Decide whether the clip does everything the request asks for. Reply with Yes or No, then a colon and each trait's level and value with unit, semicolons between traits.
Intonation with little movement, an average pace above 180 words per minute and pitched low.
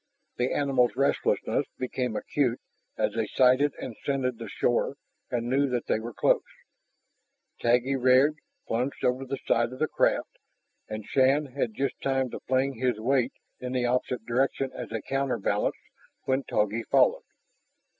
No: narrow, 2.3 semitones; average, 155 wpm; low, 125 Hz